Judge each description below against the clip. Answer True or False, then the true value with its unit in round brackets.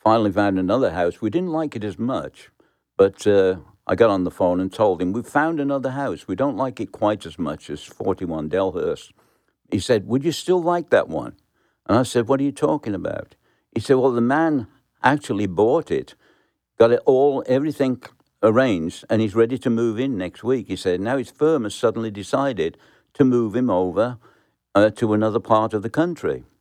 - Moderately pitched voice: False (120 Hz)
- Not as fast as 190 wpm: False (205 wpm)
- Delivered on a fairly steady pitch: False (4.6 semitones)